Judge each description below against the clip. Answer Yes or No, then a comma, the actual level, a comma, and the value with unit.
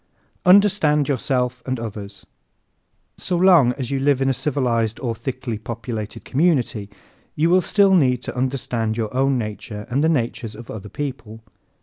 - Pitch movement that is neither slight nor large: Yes, average, 4.2 semitones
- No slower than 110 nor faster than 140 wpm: No, average, 160 wpm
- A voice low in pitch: Yes, low, 125 Hz